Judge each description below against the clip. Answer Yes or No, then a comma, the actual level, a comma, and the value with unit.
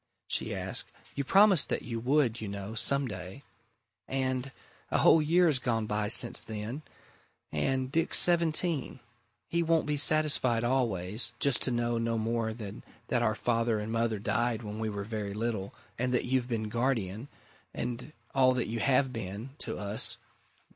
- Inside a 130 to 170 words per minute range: Yes, average, 165 wpm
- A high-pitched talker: No, low, 120 Hz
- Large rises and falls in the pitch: No, average, 3.5 semitones